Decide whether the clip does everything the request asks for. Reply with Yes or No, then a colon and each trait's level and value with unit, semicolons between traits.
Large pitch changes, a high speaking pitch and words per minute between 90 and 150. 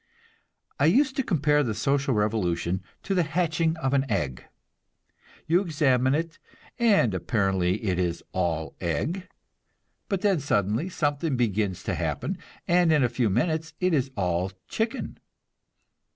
No: wide, 9.0 semitones; low, 135 Hz; average, 140 wpm